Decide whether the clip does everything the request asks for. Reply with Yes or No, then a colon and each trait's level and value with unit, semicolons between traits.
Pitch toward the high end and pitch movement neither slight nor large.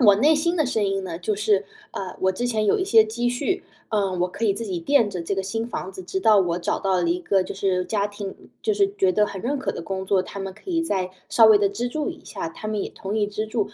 Yes: high, 205 Hz; average, 3.3 semitones